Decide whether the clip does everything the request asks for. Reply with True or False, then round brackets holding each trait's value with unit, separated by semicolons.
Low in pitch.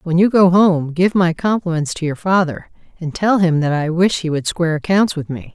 False (170 Hz)